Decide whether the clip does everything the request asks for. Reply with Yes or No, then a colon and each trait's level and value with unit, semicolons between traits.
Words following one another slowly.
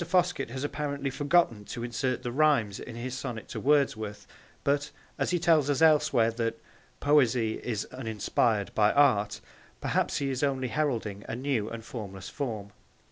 No: average, 160 wpm